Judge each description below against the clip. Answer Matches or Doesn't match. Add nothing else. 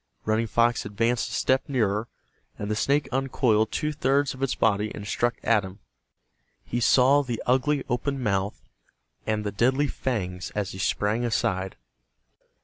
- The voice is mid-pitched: Doesn't match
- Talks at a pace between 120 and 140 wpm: Doesn't match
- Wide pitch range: Doesn't match